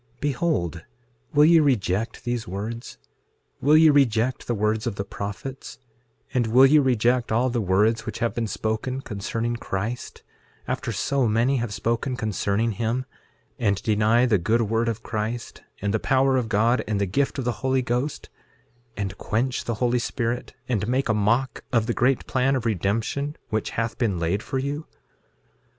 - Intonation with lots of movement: No, average, 3.2 semitones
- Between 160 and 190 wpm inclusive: Yes, average, 175 wpm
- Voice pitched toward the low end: Yes, low, 115 Hz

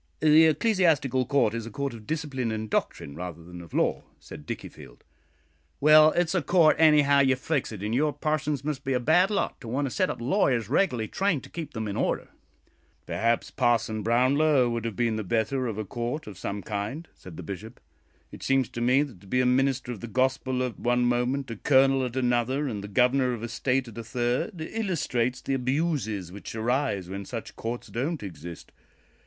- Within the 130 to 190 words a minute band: No, fast, 205 wpm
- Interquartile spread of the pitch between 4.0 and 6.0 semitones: Yes, average, 4.3 semitones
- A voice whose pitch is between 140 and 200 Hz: No, low, 125 Hz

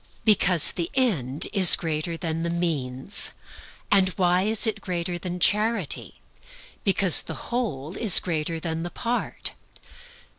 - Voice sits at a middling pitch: Yes, medium, 175 Hz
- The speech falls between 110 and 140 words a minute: Yes, slow, 135 wpm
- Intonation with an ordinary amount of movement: Yes, average, 3.8 semitones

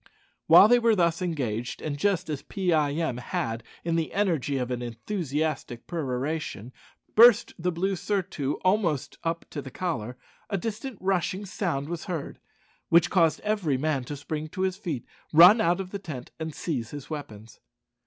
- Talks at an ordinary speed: Yes, average, 175 wpm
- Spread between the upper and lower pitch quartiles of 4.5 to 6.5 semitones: Yes, average, 5.3 semitones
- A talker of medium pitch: Yes, medium, 160 Hz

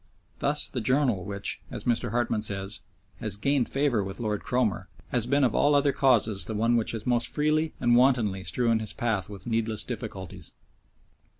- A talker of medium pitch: No, low, 115 Hz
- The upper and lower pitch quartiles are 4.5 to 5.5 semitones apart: No, average, 3.6 semitones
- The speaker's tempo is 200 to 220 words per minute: No, average, 180 wpm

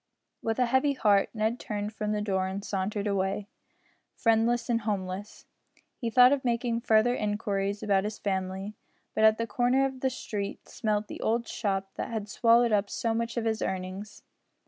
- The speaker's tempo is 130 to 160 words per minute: No, average, 180 wpm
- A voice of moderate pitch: No, high, 215 Hz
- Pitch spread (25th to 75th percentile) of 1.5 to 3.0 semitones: Yes, narrow, 2.6 semitones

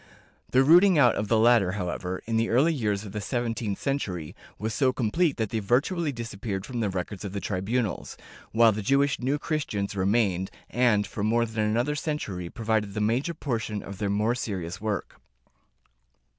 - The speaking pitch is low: Yes, low, 110 Hz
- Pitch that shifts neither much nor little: Yes, average, 4.0 semitones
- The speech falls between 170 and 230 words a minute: Yes, average, 180 wpm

